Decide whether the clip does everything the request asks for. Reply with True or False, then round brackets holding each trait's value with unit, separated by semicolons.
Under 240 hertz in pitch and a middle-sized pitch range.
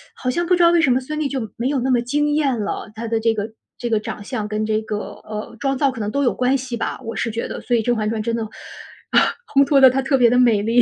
False (245 Hz; 3.4 semitones)